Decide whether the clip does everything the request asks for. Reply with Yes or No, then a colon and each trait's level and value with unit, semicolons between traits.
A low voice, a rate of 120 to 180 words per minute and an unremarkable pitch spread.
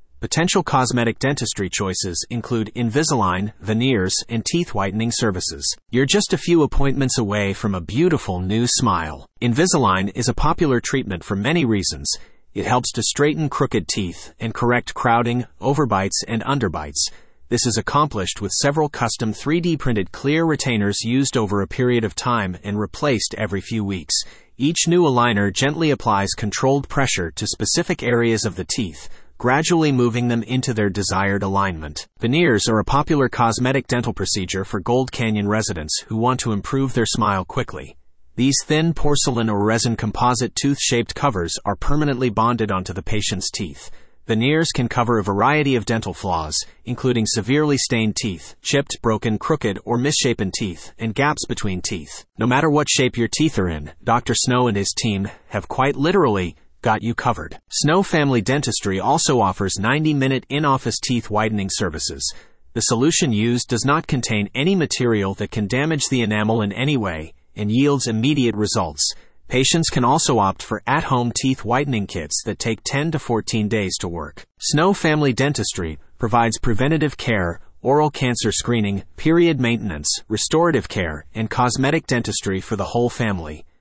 Yes: low, 115 Hz; average, 165 wpm; average, 4.8 semitones